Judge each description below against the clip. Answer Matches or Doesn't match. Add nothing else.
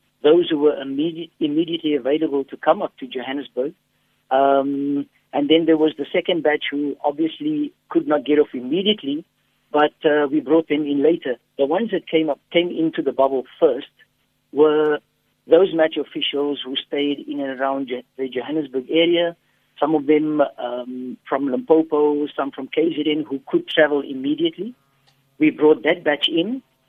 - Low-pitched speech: Doesn't match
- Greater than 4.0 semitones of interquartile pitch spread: Doesn't match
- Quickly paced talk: Doesn't match